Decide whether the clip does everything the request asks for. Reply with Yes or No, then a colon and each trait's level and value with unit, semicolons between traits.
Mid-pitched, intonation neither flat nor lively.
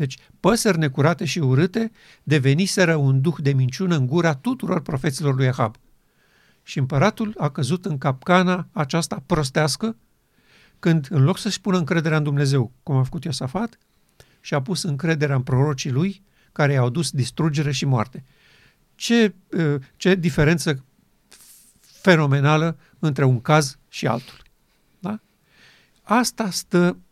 Yes: medium, 155 Hz; average, 4.7 semitones